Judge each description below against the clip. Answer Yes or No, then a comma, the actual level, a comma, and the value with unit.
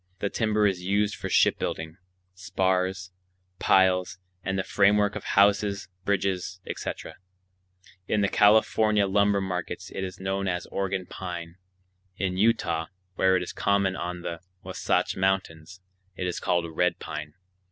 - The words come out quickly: No, average, 140 wpm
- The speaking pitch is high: No, very low, 95 Hz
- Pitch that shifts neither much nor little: No, narrow, 1.9 semitones